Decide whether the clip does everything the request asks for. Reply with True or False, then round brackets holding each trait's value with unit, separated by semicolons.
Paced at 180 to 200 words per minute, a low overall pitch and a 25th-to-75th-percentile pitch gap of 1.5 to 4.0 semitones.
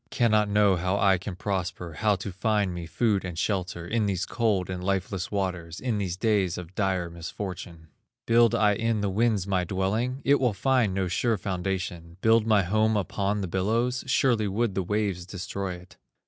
True (185 wpm; 100 Hz; 3.1 semitones)